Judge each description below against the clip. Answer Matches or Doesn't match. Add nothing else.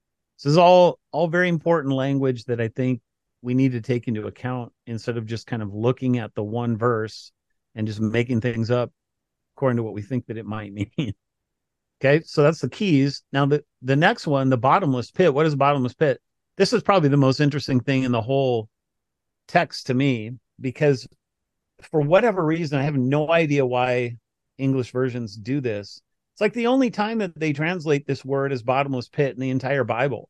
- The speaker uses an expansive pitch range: Doesn't match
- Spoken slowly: Doesn't match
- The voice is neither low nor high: Doesn't match